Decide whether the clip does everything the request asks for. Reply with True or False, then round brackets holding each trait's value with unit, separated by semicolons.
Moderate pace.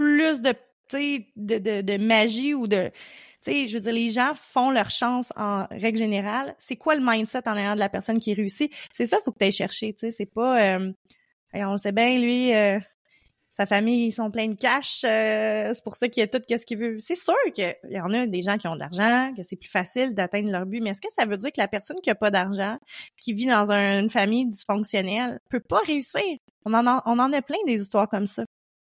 False (250 wpm)